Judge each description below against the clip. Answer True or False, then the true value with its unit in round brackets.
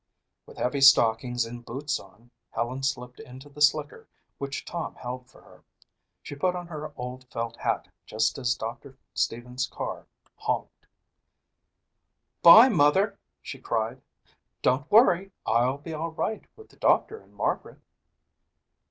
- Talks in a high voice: False (135 Hz)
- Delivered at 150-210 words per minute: False (140 wpm)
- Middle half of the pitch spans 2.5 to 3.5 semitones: False (3.9 semitones)